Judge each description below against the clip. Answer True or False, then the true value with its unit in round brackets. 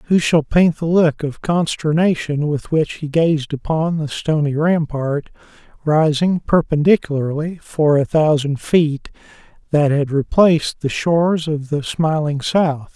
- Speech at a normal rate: False (130 wpm)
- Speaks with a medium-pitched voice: True (155 Hz)